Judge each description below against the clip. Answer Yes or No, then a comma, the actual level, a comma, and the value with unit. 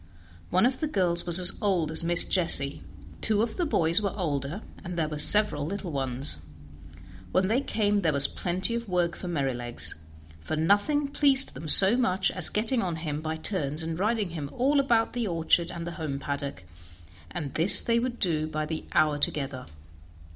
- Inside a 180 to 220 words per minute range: Yes, average, 190 wpm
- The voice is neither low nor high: Yes, medium, 175 Hz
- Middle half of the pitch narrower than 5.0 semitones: No, wide, 5.4 semitones